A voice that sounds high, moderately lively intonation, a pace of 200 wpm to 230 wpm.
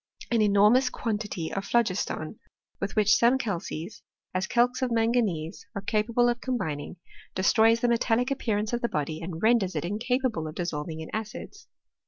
No: high, 215 Hz; average, 4.6 semitones; average, 170 wpm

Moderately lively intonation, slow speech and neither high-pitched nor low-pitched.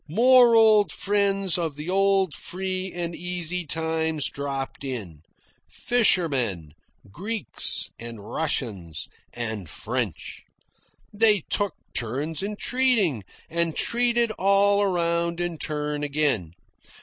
No: wide, 6.0 semitones; slow, 105 wpm; medium, 170 Hz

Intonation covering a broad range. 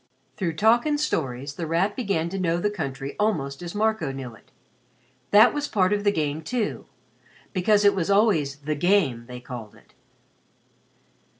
Yes: wide, 6.8 semitones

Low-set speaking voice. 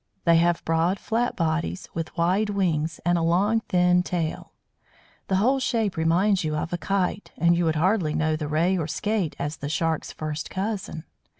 No: medium, 175 Hz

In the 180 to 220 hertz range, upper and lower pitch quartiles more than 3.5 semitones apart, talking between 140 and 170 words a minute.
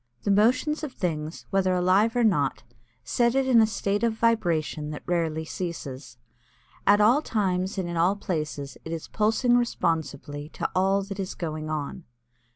Yes: medium, 185 Hz; wide, 5.5 semitones; average, 165 wpm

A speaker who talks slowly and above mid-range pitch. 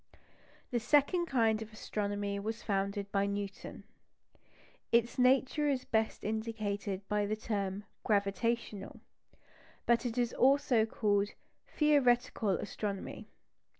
Yes: slow, 110 wpm; high, 220 Hz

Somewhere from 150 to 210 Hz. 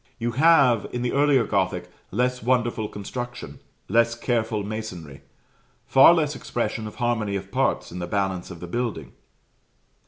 No: low, 115 Hz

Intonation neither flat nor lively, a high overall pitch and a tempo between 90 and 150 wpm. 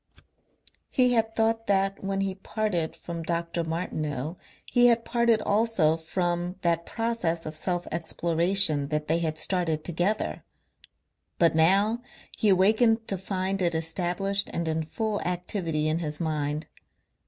No: average, 3.9 semitones; medium, 175 Hz; average, 140 wpm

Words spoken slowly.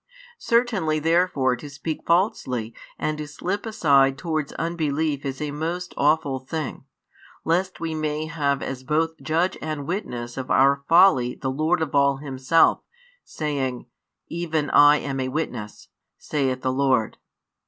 No: average, 145 wpm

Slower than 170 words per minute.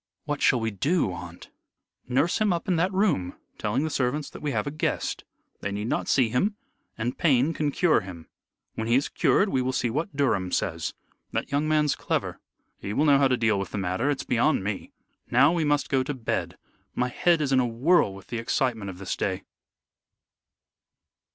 No: fast, 205 wpm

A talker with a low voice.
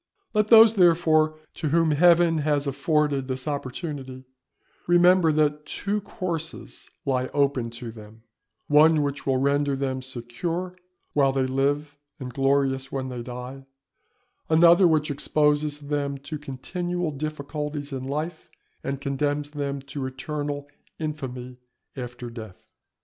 No: medium, 145 Hz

